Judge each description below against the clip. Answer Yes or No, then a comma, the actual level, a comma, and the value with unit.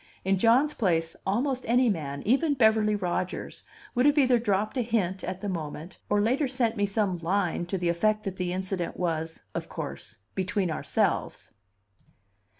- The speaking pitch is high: Yes, high, 200 Hz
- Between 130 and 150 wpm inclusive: No, average, 165 wpm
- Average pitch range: Yes, average, 4.6 semitones